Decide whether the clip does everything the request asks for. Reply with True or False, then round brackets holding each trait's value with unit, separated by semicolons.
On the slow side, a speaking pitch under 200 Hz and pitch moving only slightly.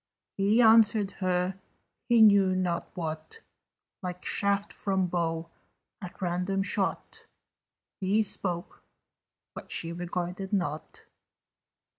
True (100 wpm; 185 Hz; 2.3 semitones)